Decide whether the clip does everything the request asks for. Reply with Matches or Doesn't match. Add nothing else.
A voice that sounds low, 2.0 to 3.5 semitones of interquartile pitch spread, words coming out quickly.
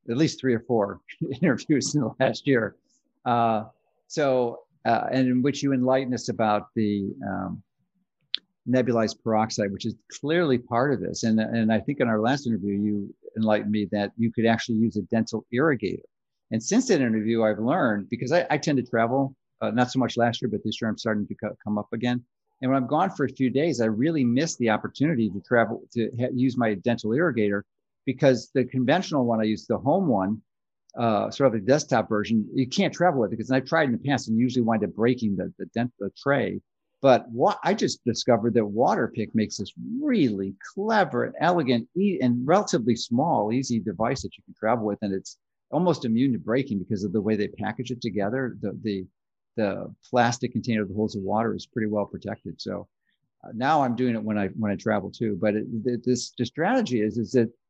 Matches